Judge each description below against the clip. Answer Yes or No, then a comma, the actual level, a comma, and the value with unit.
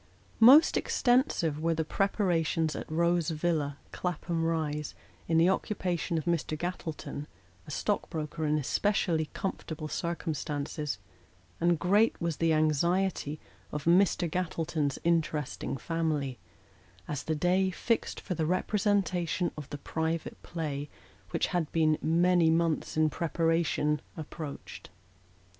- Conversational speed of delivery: No, slow, 125 wpm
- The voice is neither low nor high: Yes, medium, 165 Hz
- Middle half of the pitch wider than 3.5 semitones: No, narrow, 2.5 semitones